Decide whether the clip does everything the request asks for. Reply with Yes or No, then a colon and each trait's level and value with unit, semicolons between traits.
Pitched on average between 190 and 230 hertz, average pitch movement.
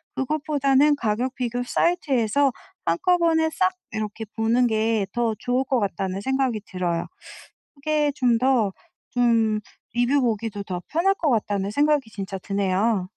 No: high, 240 Hz; average, 4.9 semitones